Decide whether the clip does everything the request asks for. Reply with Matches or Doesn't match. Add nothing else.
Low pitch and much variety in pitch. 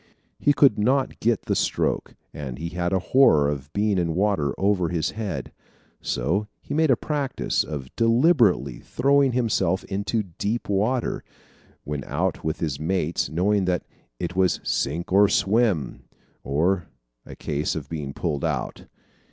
Matches